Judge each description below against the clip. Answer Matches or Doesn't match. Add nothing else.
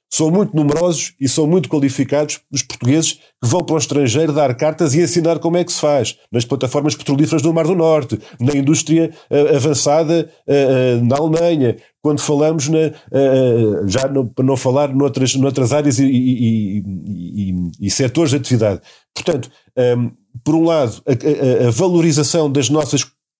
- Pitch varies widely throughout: Doesn't match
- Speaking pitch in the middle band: Matches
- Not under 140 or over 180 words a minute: Matches